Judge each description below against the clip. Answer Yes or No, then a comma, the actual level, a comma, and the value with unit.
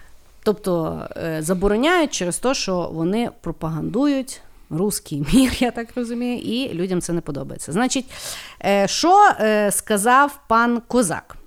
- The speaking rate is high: No, average, 115 wpm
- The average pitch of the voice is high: Yes, high, 215 Hz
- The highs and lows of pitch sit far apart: Yes, wide, 5.7 semitones